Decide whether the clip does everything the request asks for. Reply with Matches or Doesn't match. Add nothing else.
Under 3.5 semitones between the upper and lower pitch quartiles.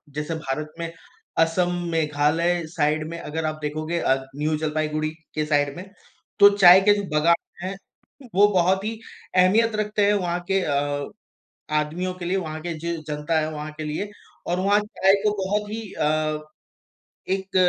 Doesn't match